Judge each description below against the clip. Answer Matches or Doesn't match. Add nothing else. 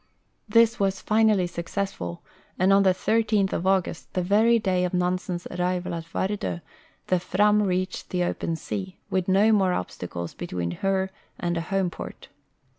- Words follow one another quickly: Doesn't match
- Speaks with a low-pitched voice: Doesn't match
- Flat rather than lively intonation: Matches